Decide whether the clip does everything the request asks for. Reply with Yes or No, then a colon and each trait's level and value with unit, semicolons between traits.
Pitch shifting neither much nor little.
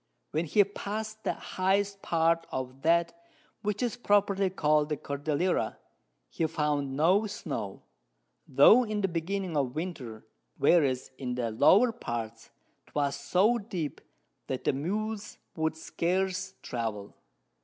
No: wide, 5.9 semitones